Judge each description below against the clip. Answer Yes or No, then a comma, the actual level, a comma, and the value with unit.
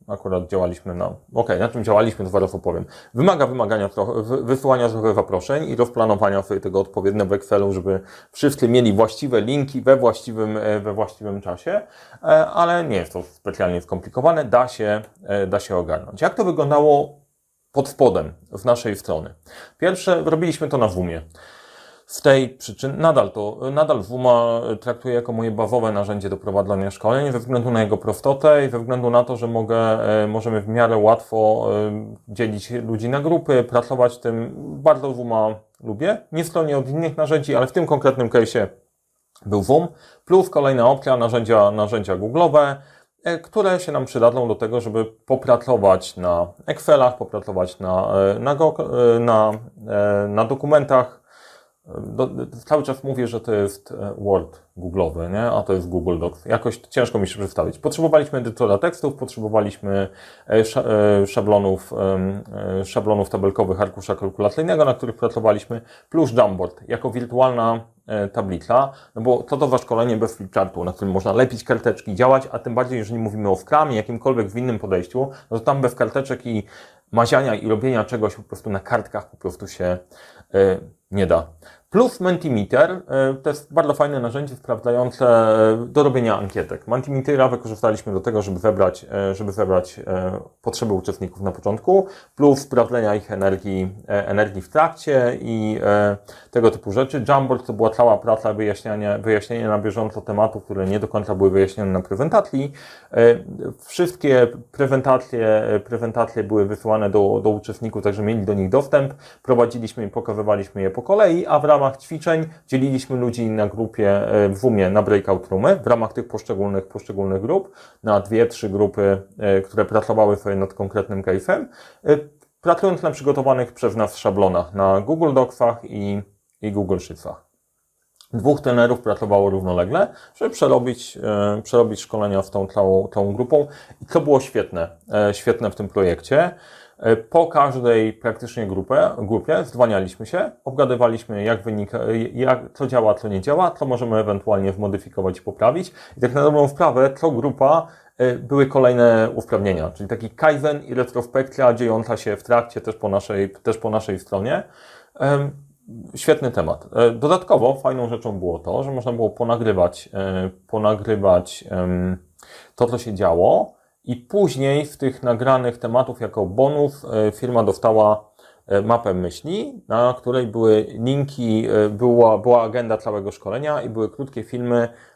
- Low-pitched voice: Yes, low, 115 Hz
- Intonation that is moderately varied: Yes, average, 4.3 semitones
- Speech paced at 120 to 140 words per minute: No, average, 150 wpm